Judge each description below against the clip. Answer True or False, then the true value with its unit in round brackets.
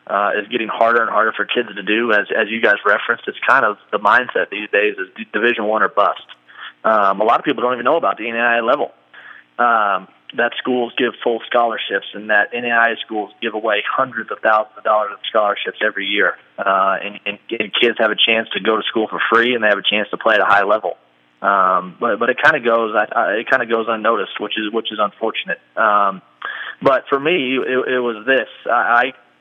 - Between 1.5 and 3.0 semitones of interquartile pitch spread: True (2.4 semitones)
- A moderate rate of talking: False (235 wpm)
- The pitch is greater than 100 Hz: True (115 Hz)